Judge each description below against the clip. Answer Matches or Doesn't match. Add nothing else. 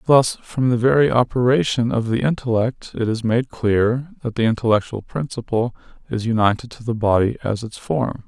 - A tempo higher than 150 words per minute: Matches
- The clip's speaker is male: Matches